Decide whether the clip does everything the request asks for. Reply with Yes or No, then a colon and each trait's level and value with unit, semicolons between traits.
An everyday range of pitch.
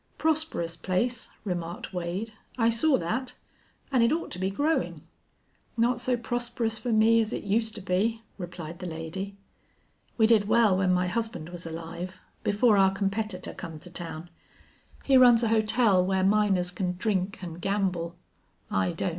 Yes: average, 4.3 semitones